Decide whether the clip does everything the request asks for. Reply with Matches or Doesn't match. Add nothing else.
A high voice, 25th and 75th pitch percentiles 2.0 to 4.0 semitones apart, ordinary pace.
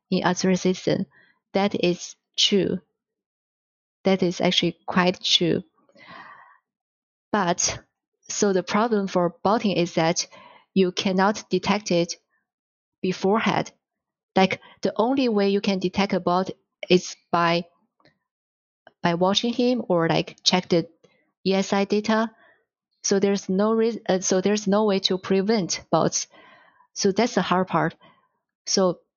Doesn't match